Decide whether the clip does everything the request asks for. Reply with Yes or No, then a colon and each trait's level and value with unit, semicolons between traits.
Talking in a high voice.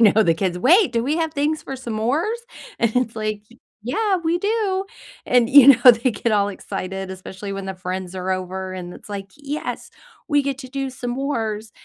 Yes: high, 235 Hz